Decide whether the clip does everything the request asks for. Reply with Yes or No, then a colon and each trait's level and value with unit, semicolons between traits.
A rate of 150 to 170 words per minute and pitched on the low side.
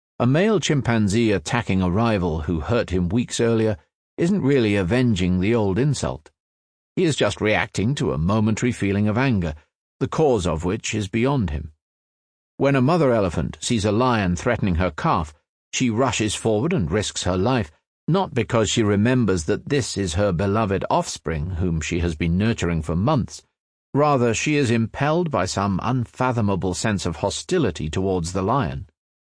Yes: average, 165 wpm; low, 105 Hz